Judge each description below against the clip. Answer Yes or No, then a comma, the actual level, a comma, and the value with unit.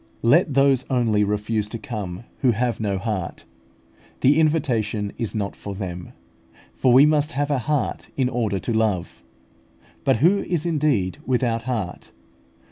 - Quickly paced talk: No, average, 150 wpm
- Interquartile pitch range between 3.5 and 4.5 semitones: No, average, 5.1 semitones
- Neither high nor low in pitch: No, low, 115 Hz